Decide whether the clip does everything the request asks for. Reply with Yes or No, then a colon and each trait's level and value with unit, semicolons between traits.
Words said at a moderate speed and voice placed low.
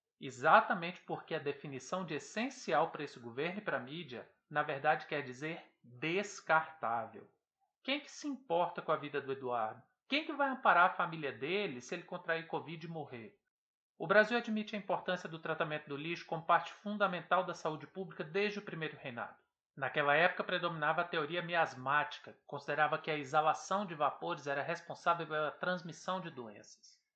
No: average, 170 wpm; medium, 165 Hz